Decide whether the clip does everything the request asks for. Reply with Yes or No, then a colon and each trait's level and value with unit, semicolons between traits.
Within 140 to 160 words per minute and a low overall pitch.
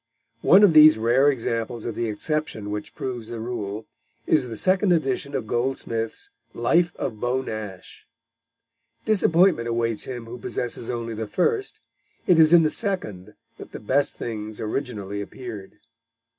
Yes: average, 150 wpm; low, 120 Hz